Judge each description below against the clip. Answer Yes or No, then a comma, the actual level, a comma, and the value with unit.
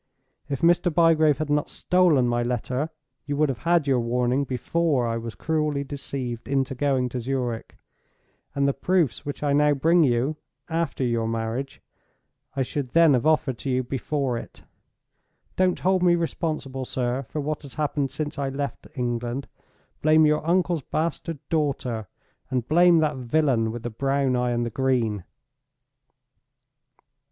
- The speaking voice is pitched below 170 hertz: Yes, medium, 140 Hz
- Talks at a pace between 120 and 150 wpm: No, average, 160 wpm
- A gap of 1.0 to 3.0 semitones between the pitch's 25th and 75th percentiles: No, average, 3.8 semitones